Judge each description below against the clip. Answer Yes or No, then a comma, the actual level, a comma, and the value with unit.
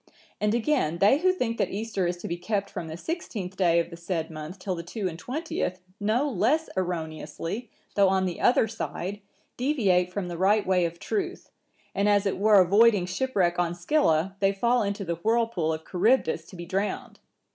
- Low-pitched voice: No, high, 195 Hz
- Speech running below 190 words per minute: No, average, 195 wpm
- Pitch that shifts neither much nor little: Yes, average, 4.6 semitones